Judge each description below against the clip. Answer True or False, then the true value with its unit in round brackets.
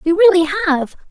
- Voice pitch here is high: True (350 Hz)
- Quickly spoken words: False (160 wpm)